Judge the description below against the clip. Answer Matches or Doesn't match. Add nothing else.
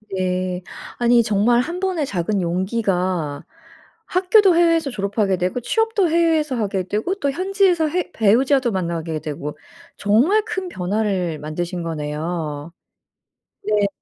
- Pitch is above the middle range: Matches